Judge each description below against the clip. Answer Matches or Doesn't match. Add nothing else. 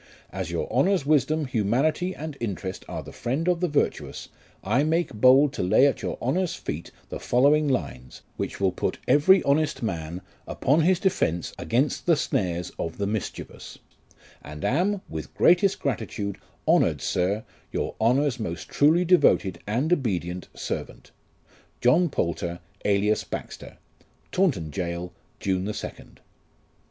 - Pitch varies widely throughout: Matches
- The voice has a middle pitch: Doesn't match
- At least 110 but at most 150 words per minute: Matches